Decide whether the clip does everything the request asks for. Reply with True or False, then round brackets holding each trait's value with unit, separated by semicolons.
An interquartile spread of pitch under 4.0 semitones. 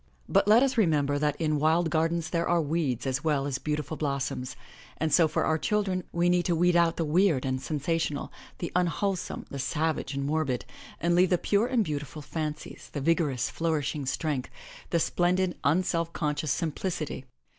True (3.1 semitones)